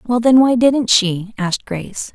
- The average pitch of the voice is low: No, high, 225 Hz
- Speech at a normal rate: Yes, average, 195 wpm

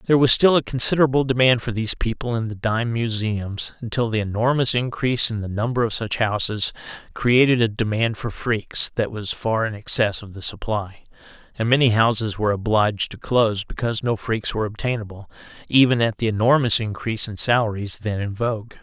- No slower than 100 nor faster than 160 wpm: No, average, 185 wpm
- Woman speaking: No, male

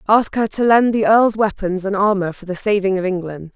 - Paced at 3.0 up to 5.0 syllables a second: No, 5.3 syllables/s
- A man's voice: No, female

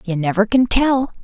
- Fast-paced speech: No, average, 195 wpm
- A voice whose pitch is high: Yes, high, 225 Hz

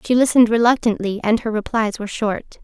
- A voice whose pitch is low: No, high, 225 Hz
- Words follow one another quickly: No, average, 185 wpm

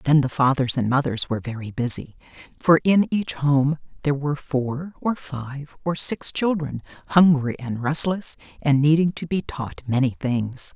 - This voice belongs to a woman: Yes, female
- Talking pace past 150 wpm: Yes, average, 165 wpm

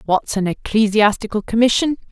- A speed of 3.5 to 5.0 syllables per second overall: No, 5.4 syllables/s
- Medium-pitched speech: No, high, 220 Hz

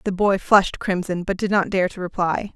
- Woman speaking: Yes, female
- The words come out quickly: Yes, fast, 235 wpm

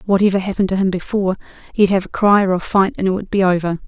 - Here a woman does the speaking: Yes, female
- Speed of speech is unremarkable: No, fast, 265 wpm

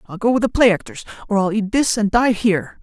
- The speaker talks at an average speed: No, fast, 275 wpm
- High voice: Yes, high, 215 Hz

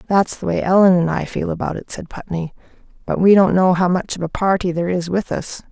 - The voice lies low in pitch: No, medium, 180 Hz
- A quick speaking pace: Yes, fast, 250 wpm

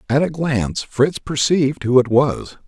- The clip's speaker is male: Yes, male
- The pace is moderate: Yes, average, 180 wpm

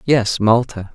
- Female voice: No, male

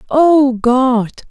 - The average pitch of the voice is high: Yes, very high, 260 Hz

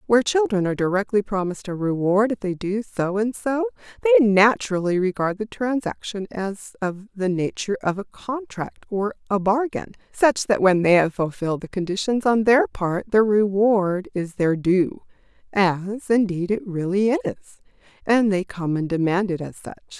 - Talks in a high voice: Yes, high, 200 Hz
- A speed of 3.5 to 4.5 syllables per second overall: No, 4.9 syllables/s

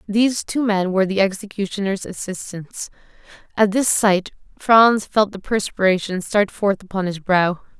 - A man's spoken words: No, female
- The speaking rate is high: No, average, 145 wpm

